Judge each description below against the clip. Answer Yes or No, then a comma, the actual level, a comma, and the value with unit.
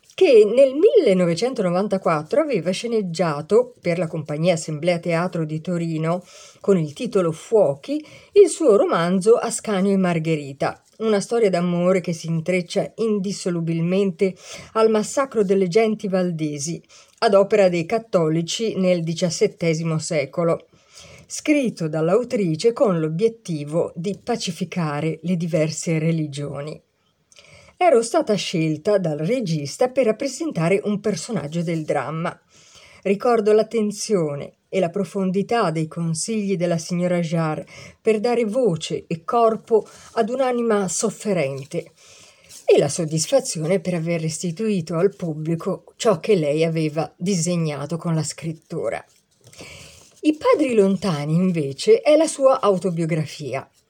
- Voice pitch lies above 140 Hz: Yes, medium, 185 Hz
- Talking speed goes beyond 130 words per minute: No, slow, 115 wpm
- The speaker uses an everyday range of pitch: Yes, average, 4.7 semitones